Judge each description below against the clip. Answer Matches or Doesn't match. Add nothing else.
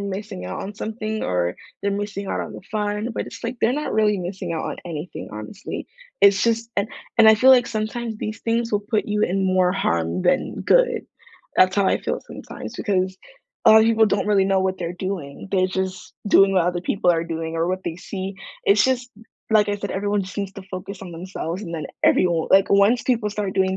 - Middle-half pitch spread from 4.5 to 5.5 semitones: Doesn't match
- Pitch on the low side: Doesn't match